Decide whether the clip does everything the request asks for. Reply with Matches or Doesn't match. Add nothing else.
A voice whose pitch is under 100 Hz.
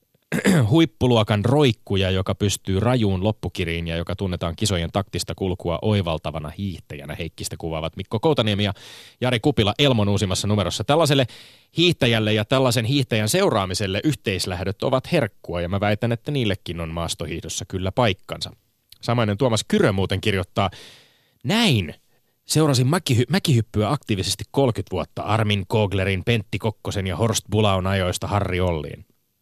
Doesn't match